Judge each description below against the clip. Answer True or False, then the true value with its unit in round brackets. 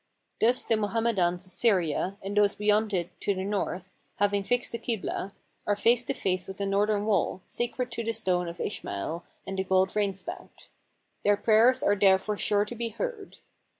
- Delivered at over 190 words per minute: False (185 wpm)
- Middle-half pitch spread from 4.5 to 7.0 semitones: False (2.9 semitones)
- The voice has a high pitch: True (205 Hz)